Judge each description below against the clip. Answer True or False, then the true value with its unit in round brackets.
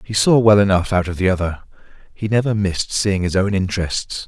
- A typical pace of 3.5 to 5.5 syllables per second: False (5.7 syllables/s)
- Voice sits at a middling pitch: False (100 Hz)